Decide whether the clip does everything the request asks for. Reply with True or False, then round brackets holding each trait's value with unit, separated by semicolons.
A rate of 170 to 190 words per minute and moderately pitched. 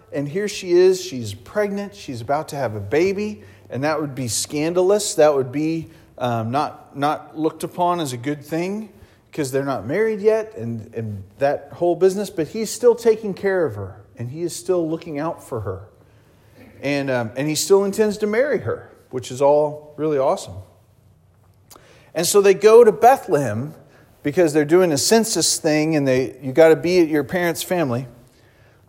True (185 wpm; 150 Hz)